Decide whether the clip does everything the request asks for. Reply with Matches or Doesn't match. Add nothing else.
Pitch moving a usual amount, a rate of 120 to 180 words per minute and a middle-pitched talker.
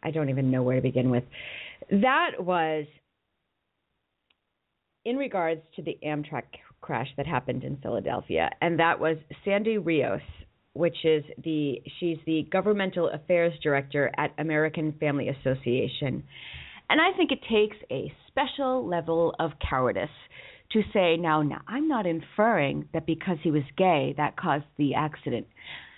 Matches